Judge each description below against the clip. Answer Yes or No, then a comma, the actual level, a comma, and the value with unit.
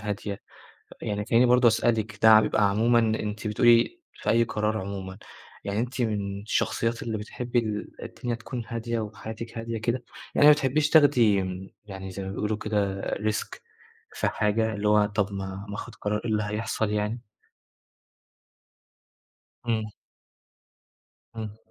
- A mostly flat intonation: Yes, narrow, 2.1 semitones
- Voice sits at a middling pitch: No, low, 110 Hz